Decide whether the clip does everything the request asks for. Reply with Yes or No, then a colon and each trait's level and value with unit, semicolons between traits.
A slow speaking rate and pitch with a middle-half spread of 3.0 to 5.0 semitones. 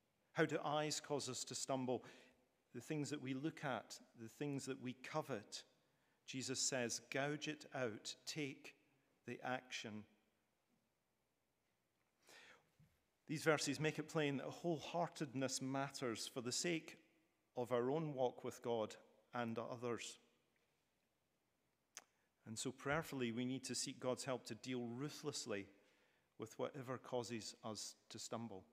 Yes: slow, 130 wpm; average, 3.4 semitones